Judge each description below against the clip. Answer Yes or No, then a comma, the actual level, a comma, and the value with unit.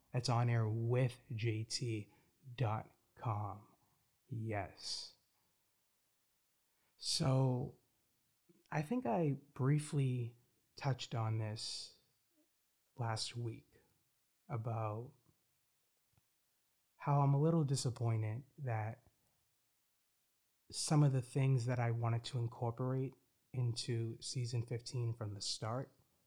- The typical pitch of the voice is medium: No, low, 120 Hz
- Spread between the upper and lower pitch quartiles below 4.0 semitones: Yes, average, 2.8 semitones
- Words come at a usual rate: No, slow, 85 wpm